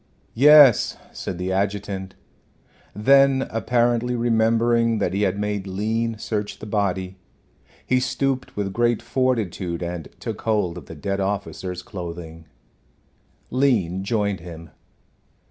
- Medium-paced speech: No, slow, 120 wpm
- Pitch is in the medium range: No, low, 105 Hz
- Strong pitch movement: No, average, 4.0 semitones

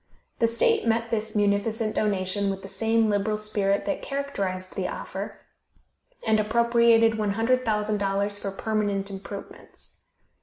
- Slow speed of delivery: Yes, slow, 120 wpm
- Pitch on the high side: Yes, high, 215 Hz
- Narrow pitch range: Yes, narrow, 2.1 semitones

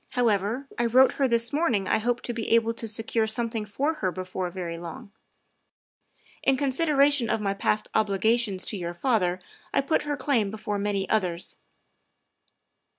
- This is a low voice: No, high, 220 Hz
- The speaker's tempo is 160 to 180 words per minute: Yes, average, 165 wpm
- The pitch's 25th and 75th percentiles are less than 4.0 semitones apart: No, average, 4.3 semitones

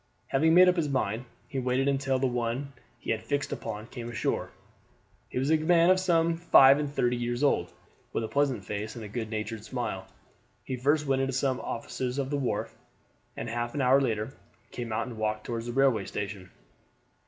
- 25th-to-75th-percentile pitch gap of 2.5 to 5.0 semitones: Yes, average, 3.5 semitones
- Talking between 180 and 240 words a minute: Yes, average, 200 wpm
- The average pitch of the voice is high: No, low, 125 Hz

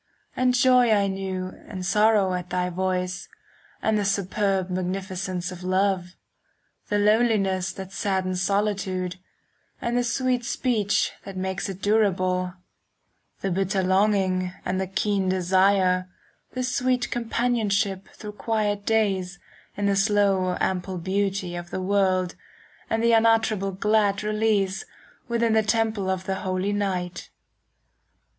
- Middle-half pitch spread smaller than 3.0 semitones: Yes, narrow, 2.4 semitones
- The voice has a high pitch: Yes, high, 195 Hz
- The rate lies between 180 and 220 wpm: No, slow, 135 wpm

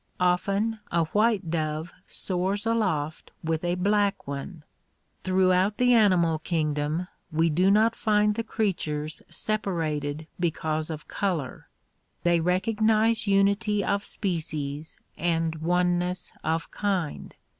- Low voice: No, medium, 180 Hz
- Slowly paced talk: Yes, slow, 120 wpm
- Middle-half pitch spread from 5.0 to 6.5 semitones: No, average, 4.3 semitones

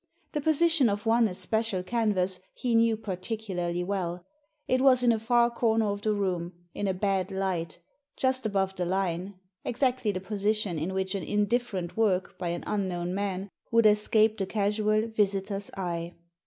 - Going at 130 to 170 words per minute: No, average, 180 wpm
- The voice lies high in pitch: Yes, high, 200 Hz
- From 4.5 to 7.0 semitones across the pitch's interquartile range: No, average, 3.3 semitones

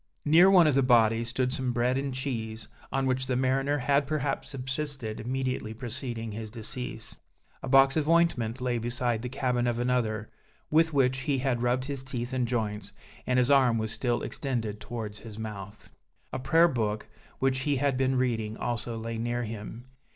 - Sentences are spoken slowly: No, average, 180 wpm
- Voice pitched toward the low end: Yes, low, 125 Hz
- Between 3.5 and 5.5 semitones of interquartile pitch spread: No, average, 2.8 semitones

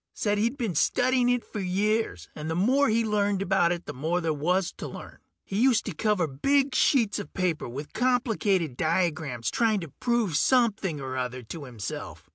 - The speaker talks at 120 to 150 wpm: No, average, 190 wpm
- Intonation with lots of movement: Yes, wide, 6.5 semitones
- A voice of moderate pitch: No, high, 195 Hz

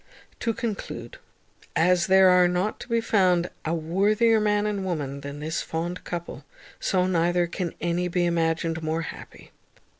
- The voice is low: No, medium, 175 Hz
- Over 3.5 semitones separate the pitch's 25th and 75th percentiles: No, average, 2.7 semitones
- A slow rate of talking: No, average, 155 wpm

